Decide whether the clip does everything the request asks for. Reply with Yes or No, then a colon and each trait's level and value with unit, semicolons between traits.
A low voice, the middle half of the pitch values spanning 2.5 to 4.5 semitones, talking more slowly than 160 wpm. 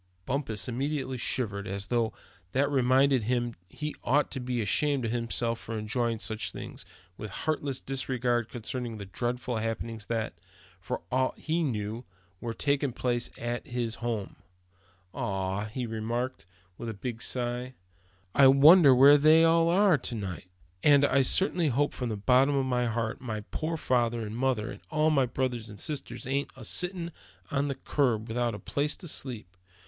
No: low, 125 Hz; average, 3.6 semitones; average, 175 wpm